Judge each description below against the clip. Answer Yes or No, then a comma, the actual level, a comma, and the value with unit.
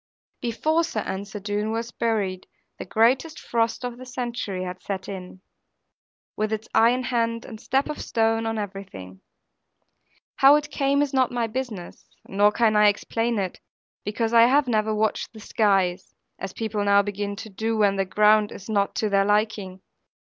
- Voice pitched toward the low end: No, high, 215 Hz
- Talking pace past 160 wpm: Yes, average, 170 wpm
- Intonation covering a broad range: No, average, 2.7 semitones